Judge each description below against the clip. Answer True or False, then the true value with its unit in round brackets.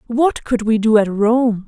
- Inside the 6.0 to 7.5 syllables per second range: False (4.0 syllables/s)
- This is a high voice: True (230 Hz)